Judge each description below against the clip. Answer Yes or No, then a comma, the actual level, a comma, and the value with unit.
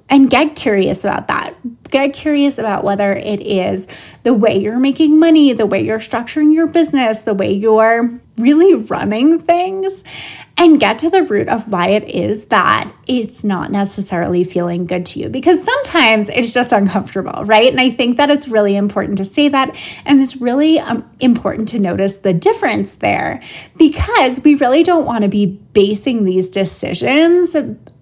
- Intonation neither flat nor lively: No, wide, 6.7 semitones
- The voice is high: Yes, high, 240 Hz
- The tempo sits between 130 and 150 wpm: No, average, 170 wpm